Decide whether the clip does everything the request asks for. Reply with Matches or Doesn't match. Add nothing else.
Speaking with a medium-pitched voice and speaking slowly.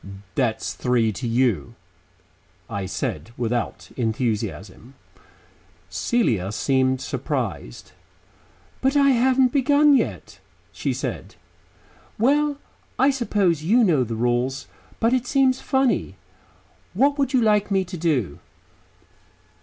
Matches